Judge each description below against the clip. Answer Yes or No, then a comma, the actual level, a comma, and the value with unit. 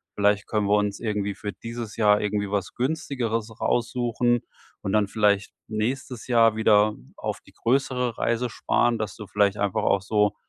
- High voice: No, low, 110 Hz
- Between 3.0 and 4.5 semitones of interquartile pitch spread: No, narrow, 2.4 semitones